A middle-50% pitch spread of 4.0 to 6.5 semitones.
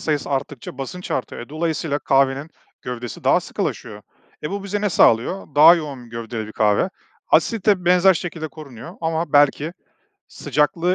Yes: average, 4.8 semitones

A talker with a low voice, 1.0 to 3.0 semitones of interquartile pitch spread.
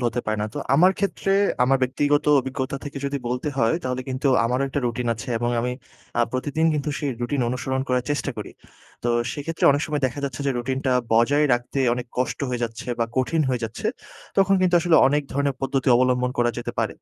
Yes: low, 130 Hz; narrow, 2.6 semitones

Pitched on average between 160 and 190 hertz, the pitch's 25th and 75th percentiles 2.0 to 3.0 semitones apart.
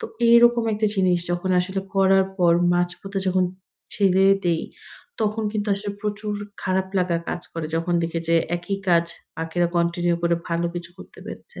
Yes: medium, 185 Hz; narrow, 2.6 semitones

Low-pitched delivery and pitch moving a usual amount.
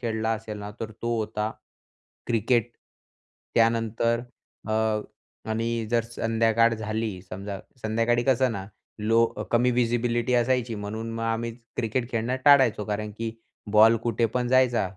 No: low, 115 Hz; narrow, 1.4 semitones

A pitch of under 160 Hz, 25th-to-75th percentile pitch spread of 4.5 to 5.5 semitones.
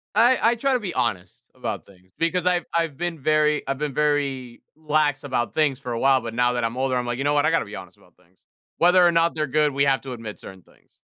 Yes: medium, 140 Hz; average, 4.9 semitones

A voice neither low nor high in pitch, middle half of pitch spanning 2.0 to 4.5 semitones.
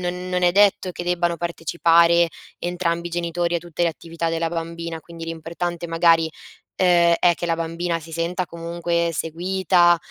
No: medium, 170 Hz; narrow, 0.8 semitones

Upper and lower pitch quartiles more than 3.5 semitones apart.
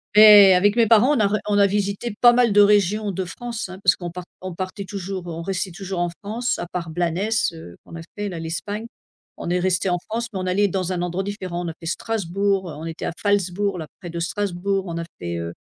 No: average, 2.8 semitones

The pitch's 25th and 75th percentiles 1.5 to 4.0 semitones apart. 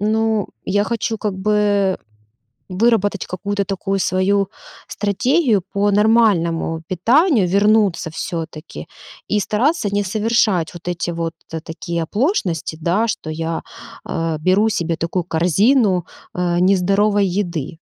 Yes: average, 3.6 semitones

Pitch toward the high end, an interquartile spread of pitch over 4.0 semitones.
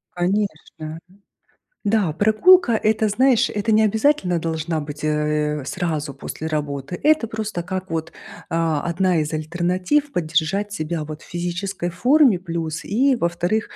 No: medium, 175 Hz; average, 5.3 semitones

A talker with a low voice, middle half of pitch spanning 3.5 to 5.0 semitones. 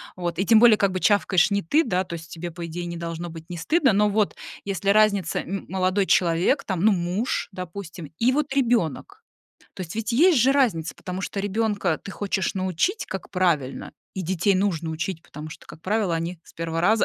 No: high, 190 Hz; average, 3.8 semitones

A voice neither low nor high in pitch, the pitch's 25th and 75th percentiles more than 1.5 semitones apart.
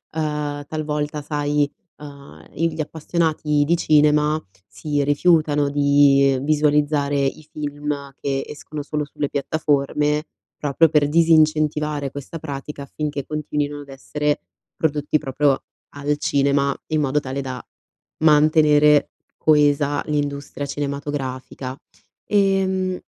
No: medium, 150 Hz; narrow, 1.2 semitones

